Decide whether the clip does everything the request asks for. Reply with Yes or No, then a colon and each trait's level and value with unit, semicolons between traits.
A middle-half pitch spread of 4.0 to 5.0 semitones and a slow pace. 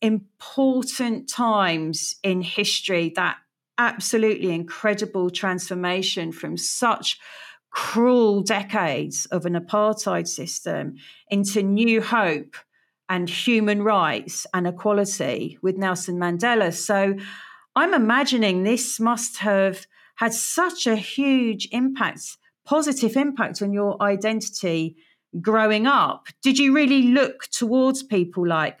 Yes: average, 4.4 semitones; slow, 110 wpm